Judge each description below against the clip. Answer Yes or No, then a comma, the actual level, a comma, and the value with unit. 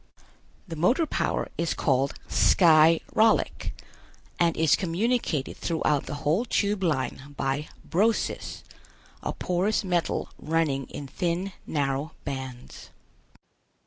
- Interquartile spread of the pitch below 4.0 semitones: No, average, 4.6 semitones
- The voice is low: No, medium, 165 Hz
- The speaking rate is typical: No, slow, 110 wpm